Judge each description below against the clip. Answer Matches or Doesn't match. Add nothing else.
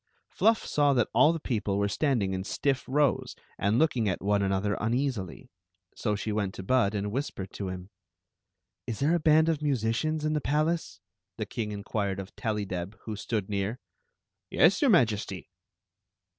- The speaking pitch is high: Doesn't match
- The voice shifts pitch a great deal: Matches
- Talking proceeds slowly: Doesn't match